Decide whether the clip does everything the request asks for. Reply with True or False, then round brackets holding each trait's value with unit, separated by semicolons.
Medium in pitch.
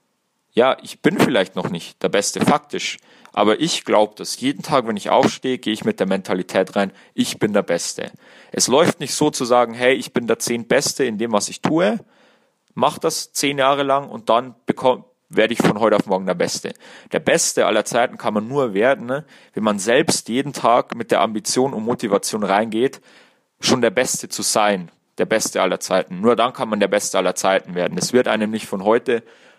False (120 Hz)